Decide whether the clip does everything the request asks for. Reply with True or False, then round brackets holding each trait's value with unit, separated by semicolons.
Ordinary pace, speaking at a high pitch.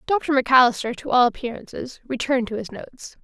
True (165 wpm; 255 Hz)